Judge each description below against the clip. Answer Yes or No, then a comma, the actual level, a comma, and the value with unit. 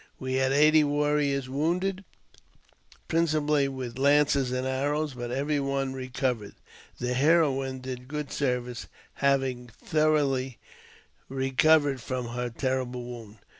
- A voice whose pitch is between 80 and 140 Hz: Yes, low, 135 Hz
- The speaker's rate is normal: No, slow, 115 wpm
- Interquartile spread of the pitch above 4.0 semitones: No, narrow, 2.6 semitones